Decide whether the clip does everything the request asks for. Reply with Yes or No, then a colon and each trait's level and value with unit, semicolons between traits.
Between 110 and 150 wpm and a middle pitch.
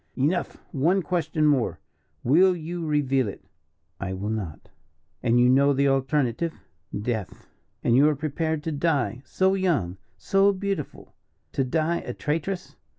Yes: average, 145 wpm; medium, 150 Hz